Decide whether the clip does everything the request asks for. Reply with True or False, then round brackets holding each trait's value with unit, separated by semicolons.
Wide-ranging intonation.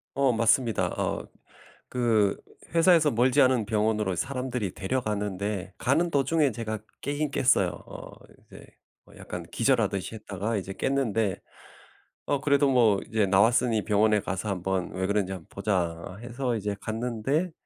False (4.6 semitones)